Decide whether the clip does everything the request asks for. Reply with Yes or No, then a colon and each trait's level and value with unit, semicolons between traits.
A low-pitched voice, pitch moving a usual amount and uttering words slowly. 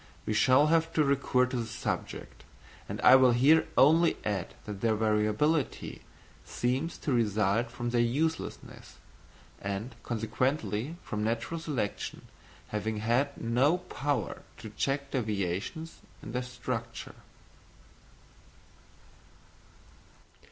Yes: low, 120 Hz; average, 4.5 semitones; slow, 110 wpm